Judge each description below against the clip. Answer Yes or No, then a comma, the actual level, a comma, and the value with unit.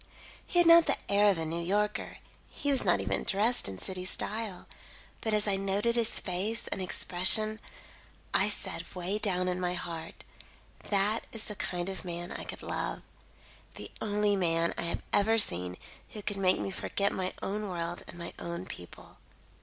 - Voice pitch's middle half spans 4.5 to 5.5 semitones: No, average, 3.2 semitones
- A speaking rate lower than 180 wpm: No, average, 185 wpm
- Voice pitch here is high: Yes, high, 195 Hz